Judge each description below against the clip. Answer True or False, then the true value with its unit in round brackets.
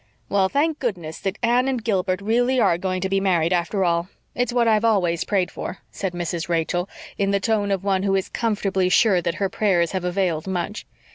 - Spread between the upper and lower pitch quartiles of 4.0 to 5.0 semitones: False (3.3 semitones)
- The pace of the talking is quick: True (210 wpm)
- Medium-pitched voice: False (195 Hz)